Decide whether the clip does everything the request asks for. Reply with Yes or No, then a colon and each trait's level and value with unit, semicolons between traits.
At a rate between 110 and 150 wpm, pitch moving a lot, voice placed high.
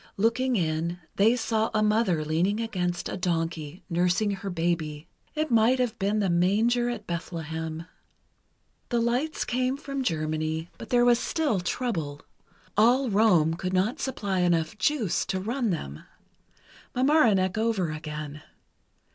Yes: average, 140 wpm; wide, 6.2 semitones; high, 195 Hz